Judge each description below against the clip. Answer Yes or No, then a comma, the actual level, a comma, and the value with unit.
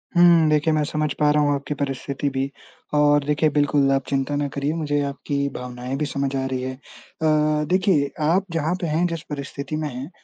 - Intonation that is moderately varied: No, narrow, 2.0 semitones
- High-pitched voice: No, medium, 145 Hz